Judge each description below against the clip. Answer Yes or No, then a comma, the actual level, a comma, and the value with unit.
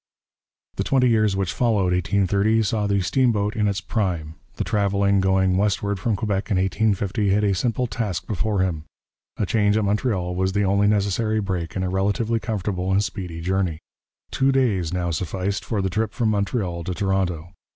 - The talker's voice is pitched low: Yes, low, 100 Hz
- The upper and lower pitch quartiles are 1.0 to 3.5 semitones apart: Yes, narrow, 2.5 semitones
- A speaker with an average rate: Yes, average, 180 wpm